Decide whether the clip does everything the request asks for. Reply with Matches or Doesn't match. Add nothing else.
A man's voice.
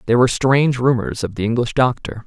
Matches